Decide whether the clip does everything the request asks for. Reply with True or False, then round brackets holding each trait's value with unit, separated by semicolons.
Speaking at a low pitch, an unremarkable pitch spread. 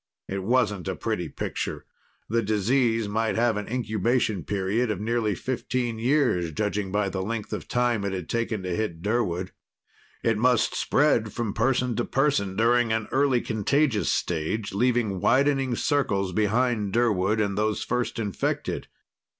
True (110 Hz; 3.3 semitones)